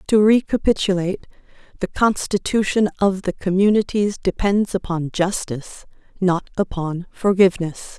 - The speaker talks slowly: Yes, slow, 100 wpm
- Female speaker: Yes, female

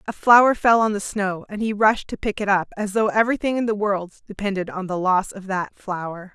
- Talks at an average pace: No, fast, 245 wpm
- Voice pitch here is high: Yes, high, 200 Hz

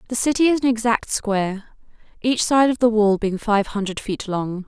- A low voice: No, high, 220 Hz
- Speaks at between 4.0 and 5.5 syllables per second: Yes, 5.0 syllables/s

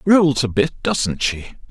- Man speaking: Yes, male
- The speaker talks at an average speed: Yes, average, 175 wpm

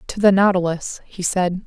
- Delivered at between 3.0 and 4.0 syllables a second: No, 4.7 syllables/s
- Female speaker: Yes, female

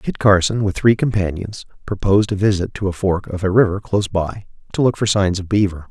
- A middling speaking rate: No, fast, 225 wpm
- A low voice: Yes, low, 100 Hz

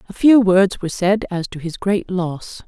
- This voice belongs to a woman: Yes, female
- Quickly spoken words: Yes, fast, 225 wpm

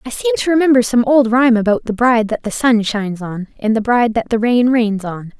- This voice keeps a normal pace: No, fast, 255 wpm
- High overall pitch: Yes, high, 235 Hz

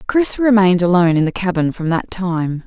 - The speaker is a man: No, female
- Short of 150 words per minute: No, average, 200 wpm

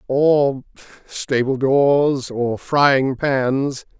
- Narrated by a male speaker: Yes, male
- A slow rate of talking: Yes, slow, 90 wpm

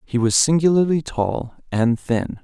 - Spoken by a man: Yes, male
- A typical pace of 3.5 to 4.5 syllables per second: Yes, 4.2 syllables/s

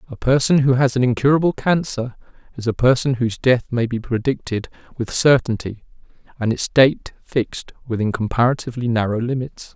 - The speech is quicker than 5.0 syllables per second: Yes, 5.5 syllables/s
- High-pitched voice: No, low, 125 Hz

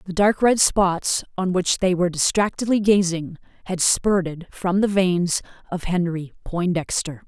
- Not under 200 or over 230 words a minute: No, average, 150 wpm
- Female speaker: Yes, female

